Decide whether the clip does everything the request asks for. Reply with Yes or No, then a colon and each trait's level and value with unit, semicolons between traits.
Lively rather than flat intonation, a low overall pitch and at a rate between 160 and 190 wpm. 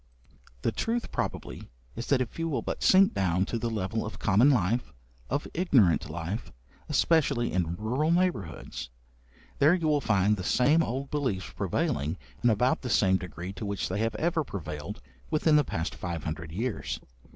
Yes: wide, 7.7 semitones; low, 110 Hz; average, 175 wpm